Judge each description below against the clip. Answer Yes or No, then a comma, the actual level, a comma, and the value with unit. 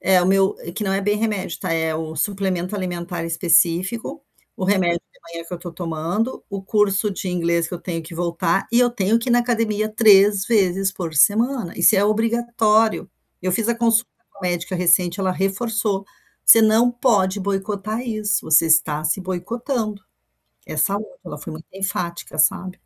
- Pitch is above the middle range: Yes, high, 195 Hz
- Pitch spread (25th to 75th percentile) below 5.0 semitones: Yes, average, 3.9 semitones